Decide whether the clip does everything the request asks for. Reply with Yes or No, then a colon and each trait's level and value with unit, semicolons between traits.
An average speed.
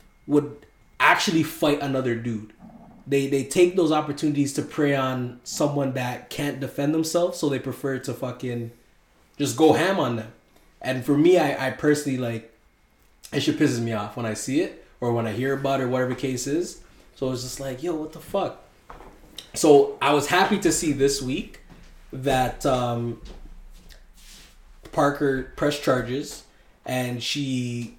Yes: average, 165 wpm